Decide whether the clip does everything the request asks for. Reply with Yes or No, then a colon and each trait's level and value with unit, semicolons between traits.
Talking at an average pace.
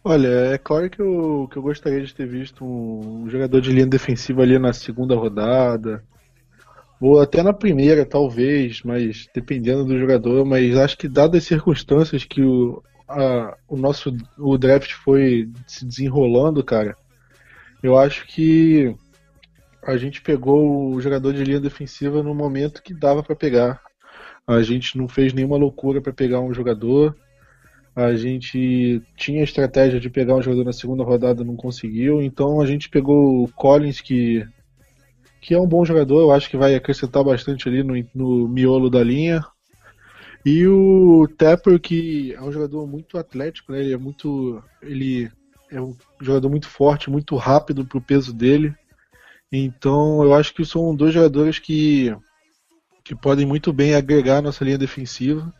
Yes: average, 165 wpm